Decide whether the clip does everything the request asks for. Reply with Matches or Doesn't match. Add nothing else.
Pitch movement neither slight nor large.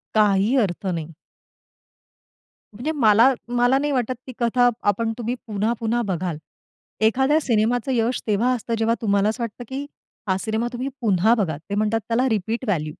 Matches